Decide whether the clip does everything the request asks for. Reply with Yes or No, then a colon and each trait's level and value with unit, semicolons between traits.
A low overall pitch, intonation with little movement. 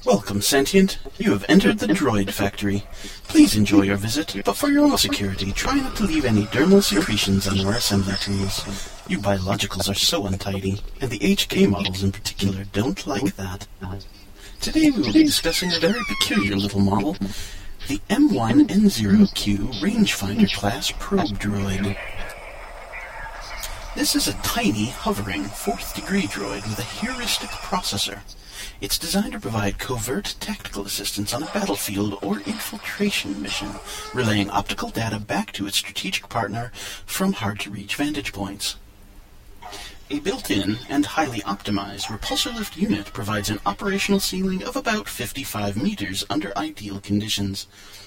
Yes: low, 100 Hz; narrow, 1.2 semitones